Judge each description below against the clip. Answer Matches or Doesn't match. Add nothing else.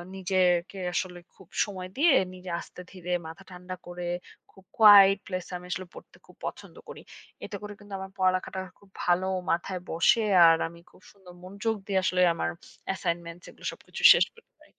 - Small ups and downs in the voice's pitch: Matches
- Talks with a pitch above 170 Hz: Matches